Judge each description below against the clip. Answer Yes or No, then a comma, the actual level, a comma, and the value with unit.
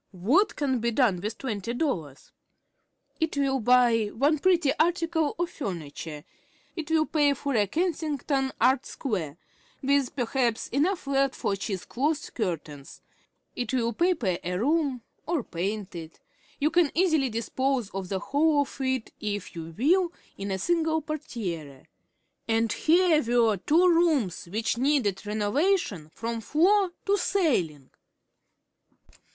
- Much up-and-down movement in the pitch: Yes, wide, 7.2 semitones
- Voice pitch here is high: Yes, very high, 260 Hz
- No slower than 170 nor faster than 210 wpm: No, slow, 135 wpm